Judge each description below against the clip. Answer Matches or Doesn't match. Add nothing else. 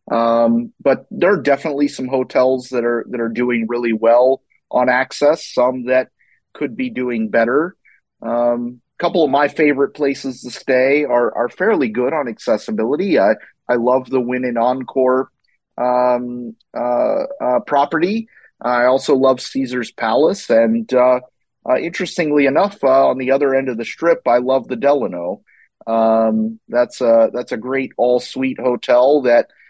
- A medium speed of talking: Matches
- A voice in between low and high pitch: Doesn't match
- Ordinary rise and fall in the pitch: Doesn't match